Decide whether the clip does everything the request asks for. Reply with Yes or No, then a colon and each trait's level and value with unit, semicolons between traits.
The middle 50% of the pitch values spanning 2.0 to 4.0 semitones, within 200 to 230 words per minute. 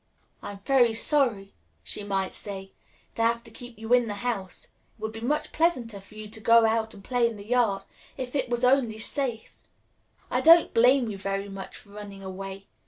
Yes: average, 3.5 semitones; fast, 205 wpm